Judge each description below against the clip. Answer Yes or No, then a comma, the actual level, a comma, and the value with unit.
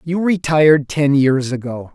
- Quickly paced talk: No, average, 155 wpm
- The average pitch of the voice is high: No, medium, 145 Hz